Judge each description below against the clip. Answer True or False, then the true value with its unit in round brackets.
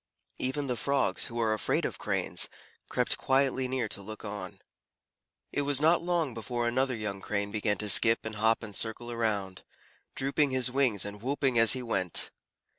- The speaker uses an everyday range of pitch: True (3.9 semitones)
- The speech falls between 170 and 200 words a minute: True (180 wpm)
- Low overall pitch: True (115 Hz)